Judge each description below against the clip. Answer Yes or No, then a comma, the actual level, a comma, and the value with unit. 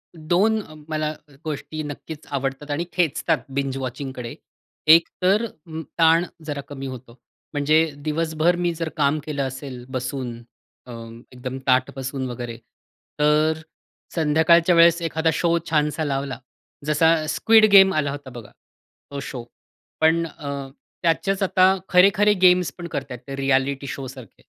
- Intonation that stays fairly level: No, average, 3.7 semitones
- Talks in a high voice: No, medium, 150 Hz